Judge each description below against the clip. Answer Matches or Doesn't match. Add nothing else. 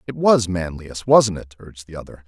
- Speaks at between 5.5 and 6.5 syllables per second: Doesn't match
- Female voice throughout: Doesn't match